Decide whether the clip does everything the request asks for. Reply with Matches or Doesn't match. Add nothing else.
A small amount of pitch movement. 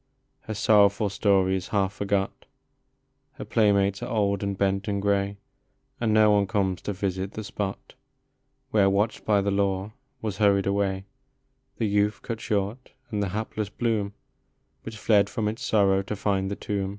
Matches